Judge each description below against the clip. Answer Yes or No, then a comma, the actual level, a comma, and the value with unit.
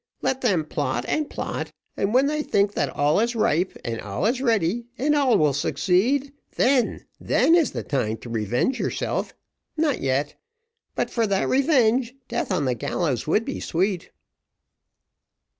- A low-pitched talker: No, high, 210 Hz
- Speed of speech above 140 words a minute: Yes, average, 160 wpm